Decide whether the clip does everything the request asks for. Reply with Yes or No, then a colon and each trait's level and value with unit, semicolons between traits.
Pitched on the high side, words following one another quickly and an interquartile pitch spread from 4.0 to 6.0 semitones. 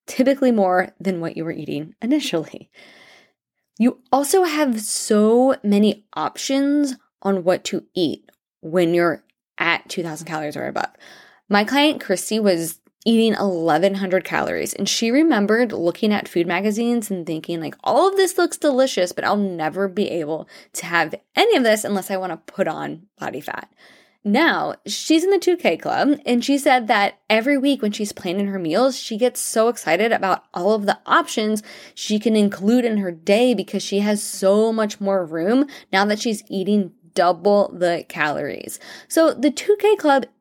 No: high, 210 Hz; average, 170 wpm; average, 5.0 semitones